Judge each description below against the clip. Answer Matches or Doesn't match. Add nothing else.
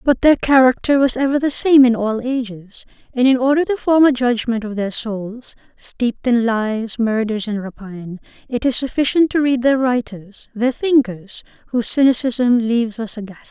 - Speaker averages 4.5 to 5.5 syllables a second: Matches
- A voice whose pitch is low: Doesn't match